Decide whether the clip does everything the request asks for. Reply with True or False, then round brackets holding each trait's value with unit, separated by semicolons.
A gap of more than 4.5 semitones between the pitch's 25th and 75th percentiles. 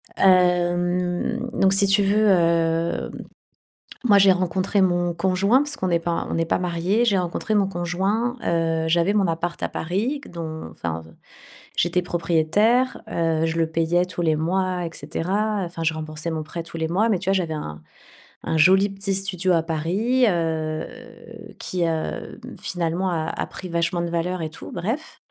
False (2.8 semitones)